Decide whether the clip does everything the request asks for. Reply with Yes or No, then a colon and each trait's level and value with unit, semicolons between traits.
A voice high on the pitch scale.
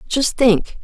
Yes: high, 240 Hz